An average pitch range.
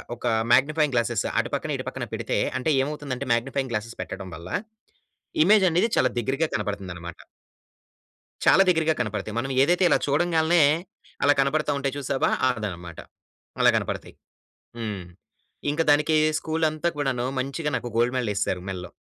No: wide, 6.1 semitones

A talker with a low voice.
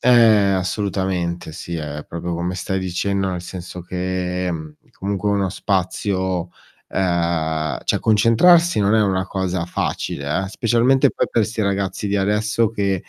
Yes: very low, 95 Hz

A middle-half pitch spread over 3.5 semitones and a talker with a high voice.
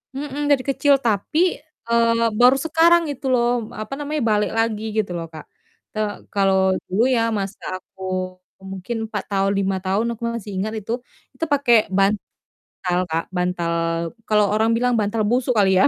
Yes: average, 4.3 semitones; high, 215 Hz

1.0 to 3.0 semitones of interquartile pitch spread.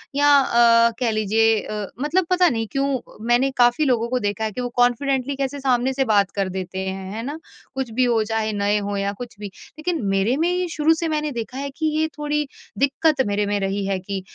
No: average, 5.1 semitones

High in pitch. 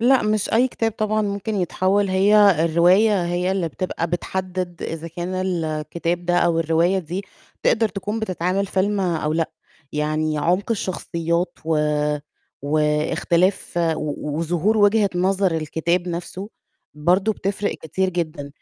No: medium, 180 Hz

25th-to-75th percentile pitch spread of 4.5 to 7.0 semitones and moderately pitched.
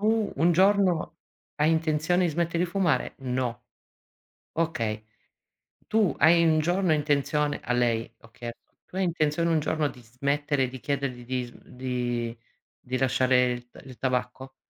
Yes: average, 5.0 semitones; medium, 145 Hz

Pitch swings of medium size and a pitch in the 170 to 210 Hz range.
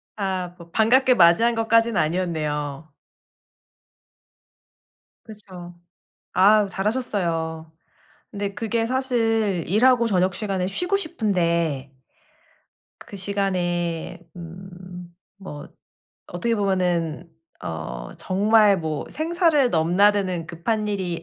Yes: average, 4.4 semitones; high, 190 Hz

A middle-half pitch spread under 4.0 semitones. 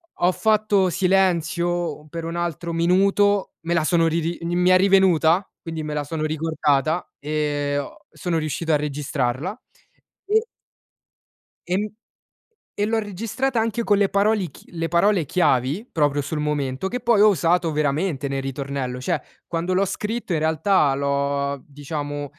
No: average, 4.7 semitones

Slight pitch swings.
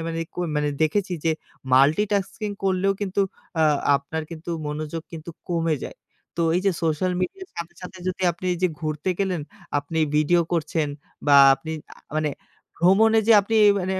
No: average, 3.5 semitones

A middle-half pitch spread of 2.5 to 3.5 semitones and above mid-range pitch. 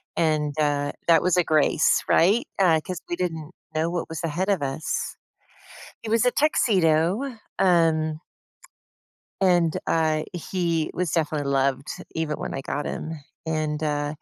No: average, 2.8 semitones; medium, 160 Hz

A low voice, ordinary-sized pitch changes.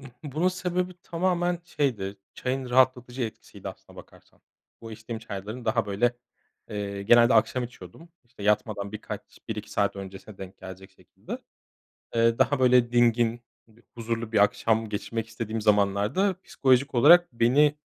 Yes: low, 115 Hz; average, 3.8 semitones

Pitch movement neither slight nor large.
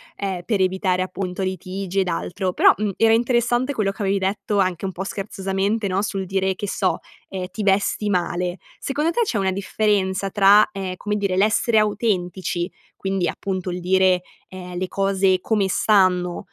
No: narrow, 1.9 semitones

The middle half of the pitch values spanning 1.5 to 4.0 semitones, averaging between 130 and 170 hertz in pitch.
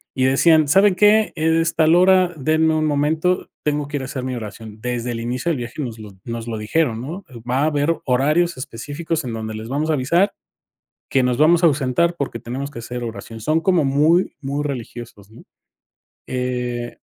No: average, 4.9 semitones; medium, 140 Hz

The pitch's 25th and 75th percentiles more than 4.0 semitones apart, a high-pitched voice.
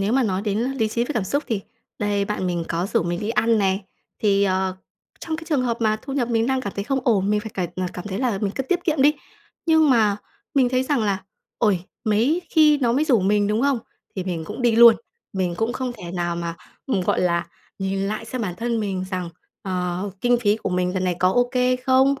Yes: average, 5.0 semitones; high, 215 Hz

